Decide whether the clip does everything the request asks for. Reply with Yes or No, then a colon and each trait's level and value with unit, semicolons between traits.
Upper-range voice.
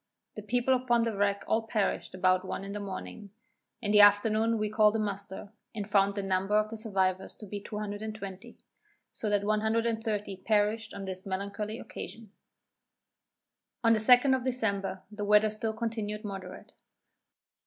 Yes: high, 210 Hz